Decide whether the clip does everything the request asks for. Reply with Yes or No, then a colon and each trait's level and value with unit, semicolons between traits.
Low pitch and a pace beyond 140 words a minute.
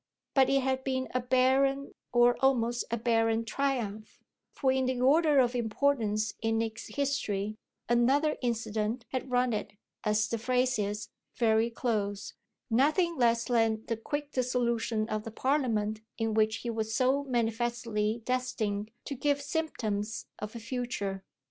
No: high, 235 Hz; average, 150 wpm